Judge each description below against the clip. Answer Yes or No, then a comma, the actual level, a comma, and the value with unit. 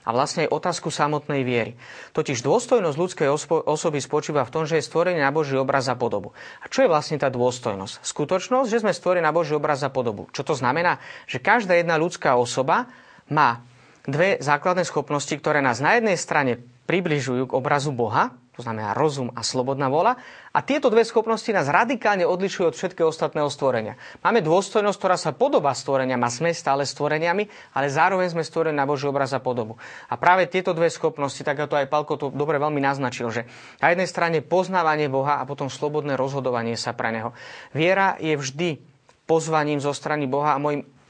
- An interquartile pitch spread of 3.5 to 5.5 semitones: Yes, average, 4.1 semitones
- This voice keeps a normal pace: No, fast, 190 wpm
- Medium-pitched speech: Yes, medium, 150 Hz